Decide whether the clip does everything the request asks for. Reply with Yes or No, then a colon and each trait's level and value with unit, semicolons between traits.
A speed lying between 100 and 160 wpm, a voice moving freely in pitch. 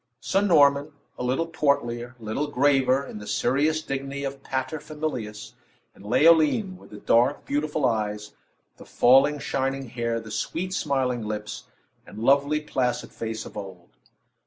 No: average, 150 wpm; average, 4.3 semitones